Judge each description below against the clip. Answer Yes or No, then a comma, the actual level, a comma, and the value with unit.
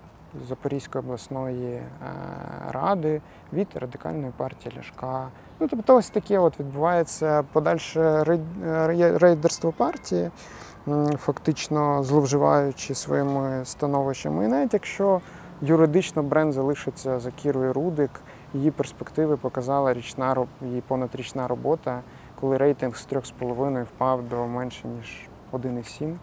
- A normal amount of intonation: Yes, average, 3.6 semitones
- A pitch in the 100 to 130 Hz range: No, medium, 140 Hz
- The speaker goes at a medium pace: No, slow, 100 wpm